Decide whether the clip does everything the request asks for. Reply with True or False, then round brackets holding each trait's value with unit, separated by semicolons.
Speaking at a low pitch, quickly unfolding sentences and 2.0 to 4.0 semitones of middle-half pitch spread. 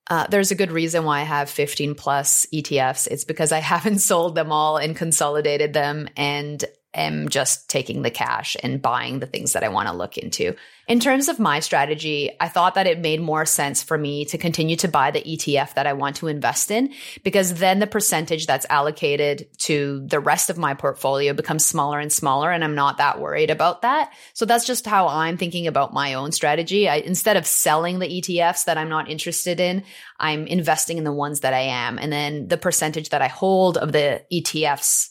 False (155 Hz; 215 wpm; 3.3 semitones)